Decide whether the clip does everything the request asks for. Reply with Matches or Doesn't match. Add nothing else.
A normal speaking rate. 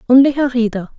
Matches